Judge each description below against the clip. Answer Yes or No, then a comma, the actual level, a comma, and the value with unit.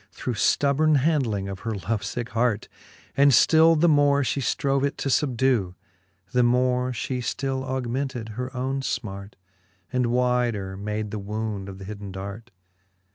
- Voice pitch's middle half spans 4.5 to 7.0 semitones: No, average, 4.1 semitones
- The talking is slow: No, average, 155 wpm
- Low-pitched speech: Yes, low, 125 Hz